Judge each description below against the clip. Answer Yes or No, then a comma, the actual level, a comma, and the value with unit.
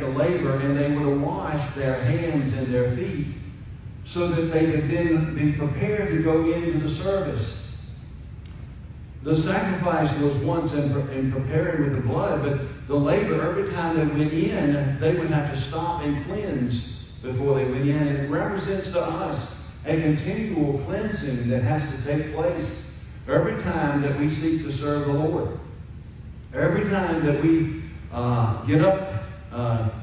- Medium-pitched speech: Yes, medium, 145 Hz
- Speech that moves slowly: No, average, 160 wpm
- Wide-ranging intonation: No, average, 3.3 semitones